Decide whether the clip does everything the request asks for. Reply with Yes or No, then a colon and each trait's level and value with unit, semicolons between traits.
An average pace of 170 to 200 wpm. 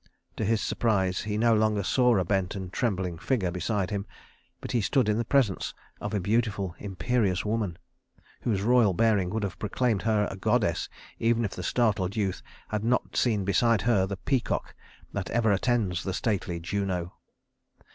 Yes: average, 175 wpm